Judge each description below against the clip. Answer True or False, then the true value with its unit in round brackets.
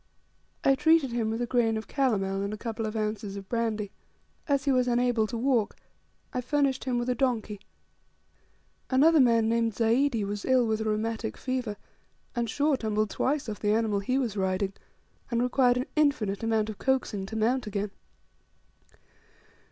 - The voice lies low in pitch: False (230 Hz)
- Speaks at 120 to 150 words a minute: False (175 wpm)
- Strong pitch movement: False (3.2 semitones)